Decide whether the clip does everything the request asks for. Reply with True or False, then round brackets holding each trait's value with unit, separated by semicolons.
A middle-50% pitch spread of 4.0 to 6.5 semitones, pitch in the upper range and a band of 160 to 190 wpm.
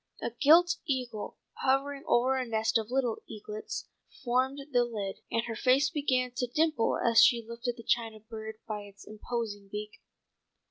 False (3.1 semitones; 235 Hz; 165 wpm)